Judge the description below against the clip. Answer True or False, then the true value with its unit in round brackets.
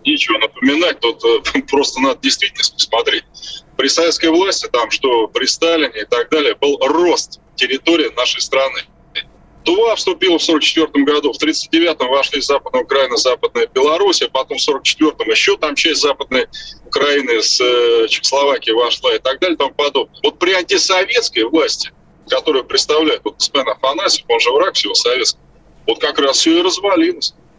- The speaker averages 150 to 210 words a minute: True (160 wpm)